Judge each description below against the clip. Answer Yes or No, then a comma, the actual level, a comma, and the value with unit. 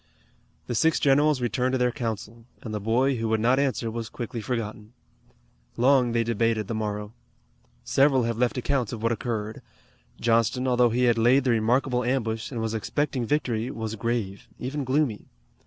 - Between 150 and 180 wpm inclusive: Yes, average, 170 wpm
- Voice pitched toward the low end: Yes, low, 120 Hz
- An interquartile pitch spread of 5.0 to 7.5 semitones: No, narrow, 2.4 semitones